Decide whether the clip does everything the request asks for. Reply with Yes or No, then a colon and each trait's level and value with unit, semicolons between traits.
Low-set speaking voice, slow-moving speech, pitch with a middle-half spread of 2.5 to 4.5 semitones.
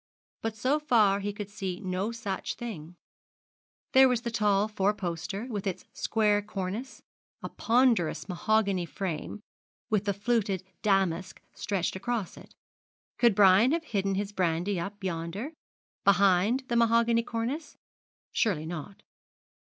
No: high, 205 Hz; slow, 130 wpm; average, 3.5 semitones